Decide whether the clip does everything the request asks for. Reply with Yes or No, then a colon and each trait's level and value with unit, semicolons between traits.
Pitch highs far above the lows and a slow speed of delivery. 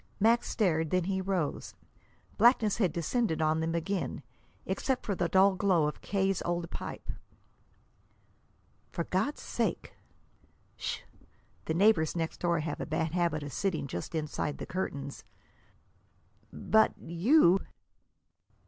No: average, 3.6 semitones; slow, 130 wpm